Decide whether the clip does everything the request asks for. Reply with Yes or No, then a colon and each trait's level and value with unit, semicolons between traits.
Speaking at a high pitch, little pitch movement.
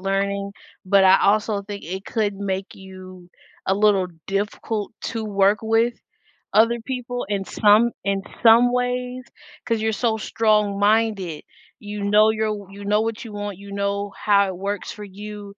Yes: high, 205 Hz; narrow, 1.9 semitones